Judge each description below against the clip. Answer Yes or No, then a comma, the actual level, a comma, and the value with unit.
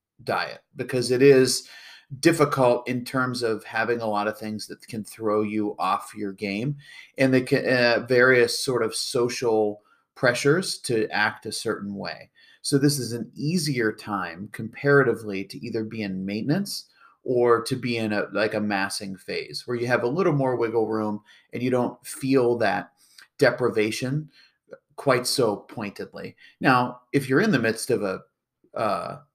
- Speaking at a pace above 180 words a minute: No, average, 165 wpm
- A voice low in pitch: Yes, low, 120 Hz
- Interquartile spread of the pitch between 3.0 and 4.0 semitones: Yes, average, 3.6 semitones